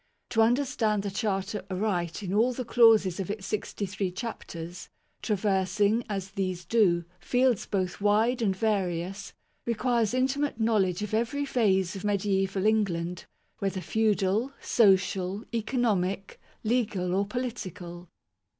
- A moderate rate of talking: No, slow, 130 wpm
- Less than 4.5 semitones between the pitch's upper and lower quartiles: Yes, average, 3.1 semitones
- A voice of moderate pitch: No, high, 205 Hz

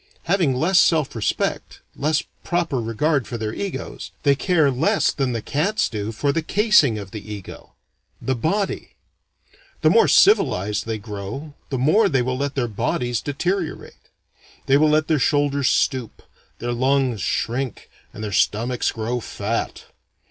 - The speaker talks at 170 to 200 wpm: No, average, 155 wpm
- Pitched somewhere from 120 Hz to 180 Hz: Yes, low, 135 Hz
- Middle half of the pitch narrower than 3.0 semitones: No, wide, 5.4 semitones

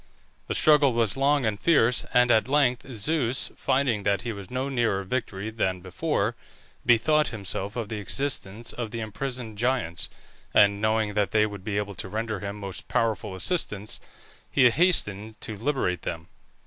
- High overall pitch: No, low, 110 Hz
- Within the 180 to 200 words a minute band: No, average, 165 wpm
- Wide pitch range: No, average, 3.9 semitones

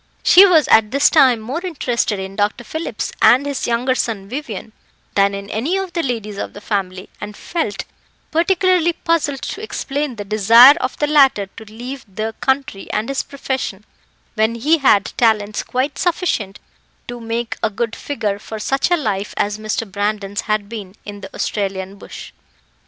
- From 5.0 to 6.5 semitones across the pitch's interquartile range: Yes, wide, 5.4 semitones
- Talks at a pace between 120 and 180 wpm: Yes, average, 175 wpm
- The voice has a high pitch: Yes, high, 230 Hz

